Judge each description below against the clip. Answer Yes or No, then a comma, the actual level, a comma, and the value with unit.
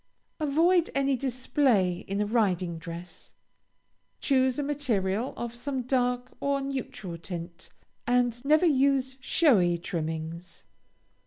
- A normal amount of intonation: No, wide, 7.1 semitones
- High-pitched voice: Yes, high, 245 Hz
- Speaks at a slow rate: Yes, slow, 110 wpm